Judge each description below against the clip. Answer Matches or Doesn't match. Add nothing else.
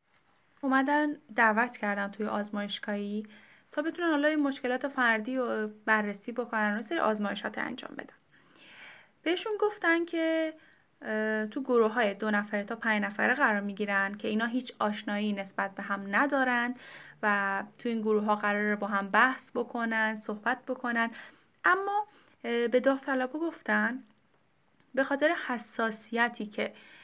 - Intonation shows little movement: Doesn't match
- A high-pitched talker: Matches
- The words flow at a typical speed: Matches